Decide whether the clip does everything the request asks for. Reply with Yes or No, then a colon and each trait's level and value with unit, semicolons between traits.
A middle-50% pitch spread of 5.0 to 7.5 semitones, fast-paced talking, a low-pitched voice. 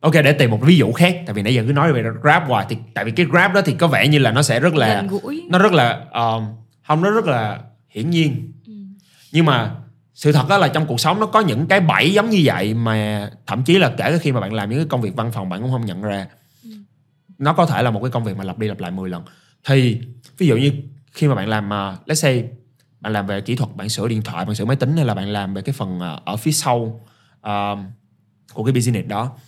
Yes: wide, 5.6 semitones; fast, 270 wpm; low, 130 Hz